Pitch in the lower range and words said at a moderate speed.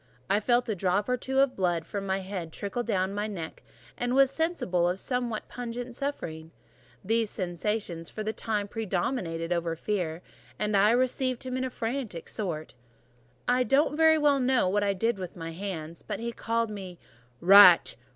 No: high, 210 Hz; average, 175 wpm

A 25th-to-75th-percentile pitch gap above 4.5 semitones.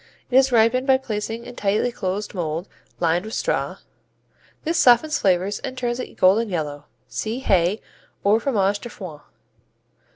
Yes: average, 4.9 semitones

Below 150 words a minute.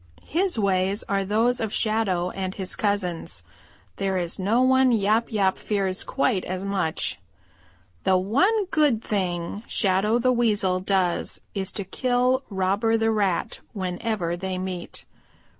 Yes: average, 140 wpm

